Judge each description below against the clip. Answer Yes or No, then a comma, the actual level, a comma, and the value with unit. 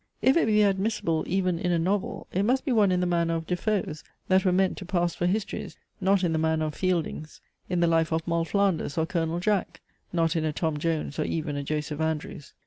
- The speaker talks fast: Yes, fast, 235 wpm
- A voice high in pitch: No, medium, 175 Hz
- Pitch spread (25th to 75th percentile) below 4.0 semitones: Yes, average, 3.1 semitones